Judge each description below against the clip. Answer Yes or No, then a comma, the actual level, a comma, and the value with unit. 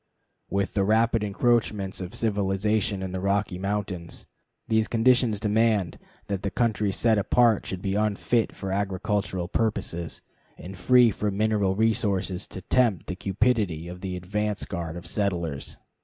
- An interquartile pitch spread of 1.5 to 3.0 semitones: Yes, average, 2.7 semitones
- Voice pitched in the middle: No, low, 100 Hz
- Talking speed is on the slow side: No, average, 145 wpm